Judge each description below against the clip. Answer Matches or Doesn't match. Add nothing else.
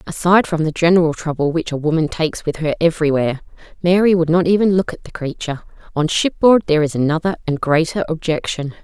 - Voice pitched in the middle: Matches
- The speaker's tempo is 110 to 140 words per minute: Doesn't match